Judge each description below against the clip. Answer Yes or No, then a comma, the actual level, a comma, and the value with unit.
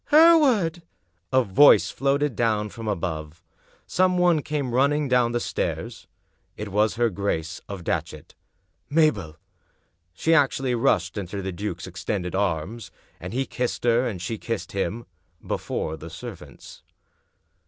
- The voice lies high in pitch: No, low, 115 Hz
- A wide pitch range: Yes, wide, 6.8 semitones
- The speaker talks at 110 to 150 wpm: Yes, average, 145 wpm